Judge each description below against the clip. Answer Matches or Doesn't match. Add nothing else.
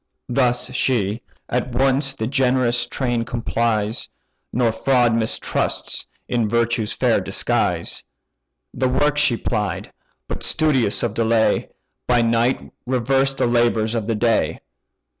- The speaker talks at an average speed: Doesn't match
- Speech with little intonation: Matches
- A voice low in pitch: Matches